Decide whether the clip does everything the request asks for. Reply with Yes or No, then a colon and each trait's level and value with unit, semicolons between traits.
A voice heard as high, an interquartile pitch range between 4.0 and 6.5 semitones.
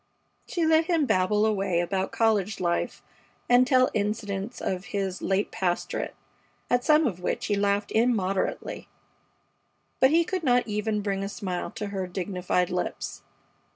Yes: high, 205 Hz; average, 4.5 semitones